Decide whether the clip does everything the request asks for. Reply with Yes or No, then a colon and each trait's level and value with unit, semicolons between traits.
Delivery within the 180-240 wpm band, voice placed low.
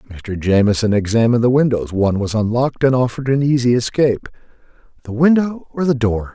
No: average, 170 wpm; low, 120 Hz